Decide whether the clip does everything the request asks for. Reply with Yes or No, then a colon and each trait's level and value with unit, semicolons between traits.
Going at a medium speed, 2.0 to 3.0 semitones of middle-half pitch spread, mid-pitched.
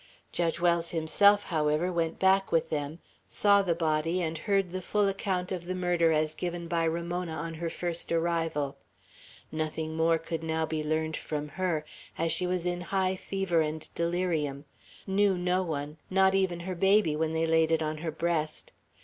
Yes: average, 180 wpm; narrow, 2.4 semitones; medium, 170 Hz